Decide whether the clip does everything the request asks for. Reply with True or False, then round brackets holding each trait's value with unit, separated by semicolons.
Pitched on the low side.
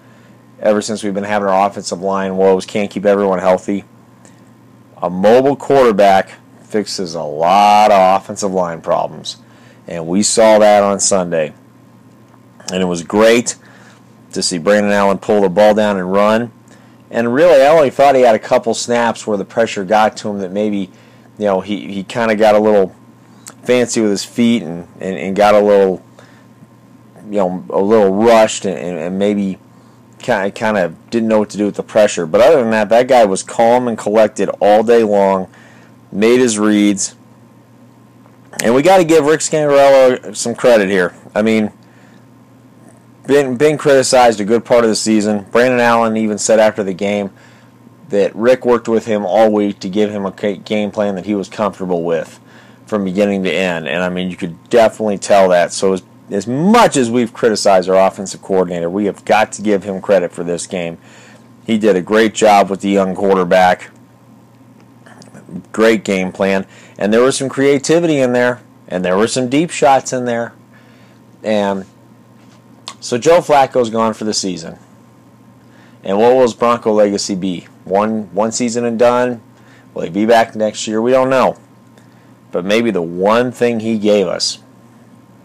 True (105 Hz)